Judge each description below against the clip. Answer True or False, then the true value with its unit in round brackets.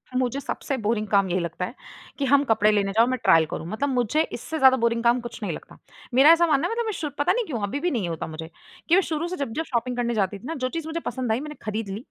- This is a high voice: True (245 Hz)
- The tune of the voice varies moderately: False (5.7 semitones)